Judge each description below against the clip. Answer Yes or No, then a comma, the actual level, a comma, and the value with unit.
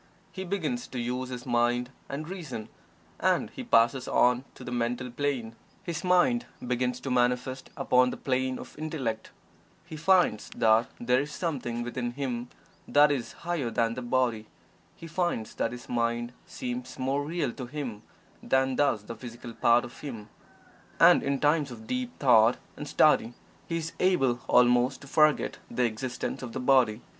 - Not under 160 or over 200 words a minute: Yes, average, 170 wpm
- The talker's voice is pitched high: No, low, 125 Hz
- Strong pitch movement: No, average, 3.4 semitones